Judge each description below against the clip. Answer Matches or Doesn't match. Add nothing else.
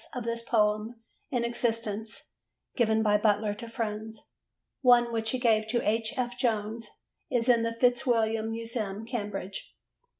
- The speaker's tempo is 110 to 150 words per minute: Matches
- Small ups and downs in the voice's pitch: Matches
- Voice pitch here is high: Matches